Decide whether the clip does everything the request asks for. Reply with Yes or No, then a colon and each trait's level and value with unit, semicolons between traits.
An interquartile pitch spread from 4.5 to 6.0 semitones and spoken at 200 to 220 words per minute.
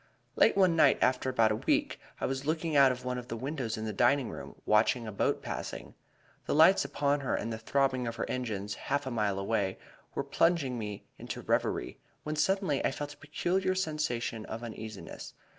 Yes: average, 4.8 semitones; fast, 205 wpm